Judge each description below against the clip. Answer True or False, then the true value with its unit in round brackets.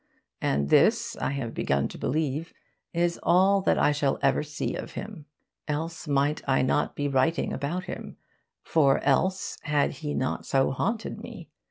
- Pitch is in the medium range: True (150 Hz)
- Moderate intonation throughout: True (3.6 semitones)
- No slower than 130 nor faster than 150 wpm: False (165 wpm)